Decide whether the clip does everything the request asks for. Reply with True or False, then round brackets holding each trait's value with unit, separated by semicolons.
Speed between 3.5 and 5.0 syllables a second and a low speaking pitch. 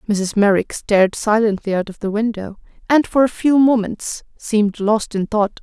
False (4.7 syllables/s; 215 Hz)